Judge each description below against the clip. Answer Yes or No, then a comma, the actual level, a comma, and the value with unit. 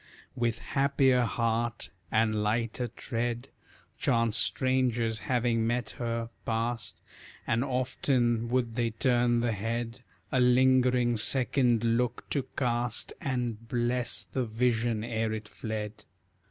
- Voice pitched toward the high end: No, low, 120 Hz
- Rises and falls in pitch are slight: Yes, narrow, 1.5 semitones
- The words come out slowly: Yes, slow, 115 wpm